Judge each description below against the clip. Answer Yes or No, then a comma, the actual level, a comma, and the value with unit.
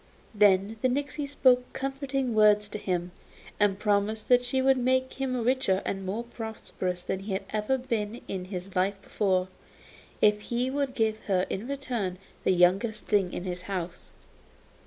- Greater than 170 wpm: No, average, 165 wpm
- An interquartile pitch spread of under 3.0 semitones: No, average, 4.9 semitones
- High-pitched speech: Yes, high, 215 Hz